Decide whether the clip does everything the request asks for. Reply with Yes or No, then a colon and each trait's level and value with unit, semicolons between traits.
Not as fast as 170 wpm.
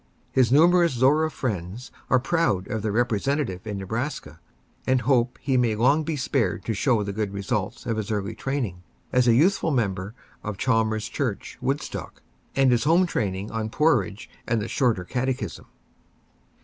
Yes: average, 160 wpm